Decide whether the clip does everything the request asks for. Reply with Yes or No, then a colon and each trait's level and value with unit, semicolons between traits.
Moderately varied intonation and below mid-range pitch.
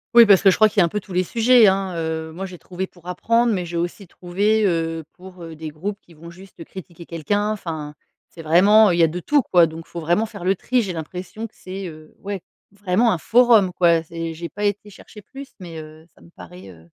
No: average, 3.7 semitones; medium, 180 Hz